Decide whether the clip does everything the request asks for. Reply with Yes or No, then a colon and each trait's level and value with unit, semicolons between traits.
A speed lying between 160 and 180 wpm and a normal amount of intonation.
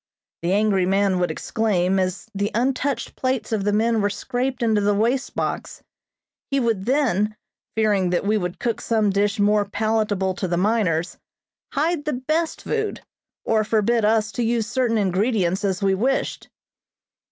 Yes: average, 165 wpm; average, 3.2 semitones